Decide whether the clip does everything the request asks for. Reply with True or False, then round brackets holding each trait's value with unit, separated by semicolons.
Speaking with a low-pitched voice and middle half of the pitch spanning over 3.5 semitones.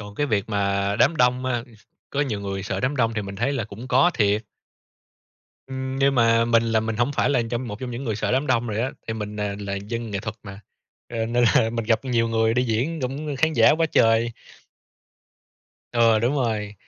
False (115 Hz; 3.2 semitones)